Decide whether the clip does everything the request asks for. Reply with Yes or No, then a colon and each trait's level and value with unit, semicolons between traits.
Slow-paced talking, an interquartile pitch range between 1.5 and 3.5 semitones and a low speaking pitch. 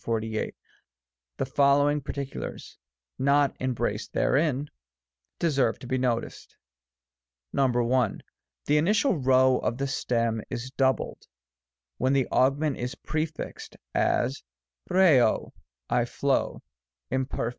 Yes: slow, 105 wpm; average, 3.1 semitones; low, 130 Hz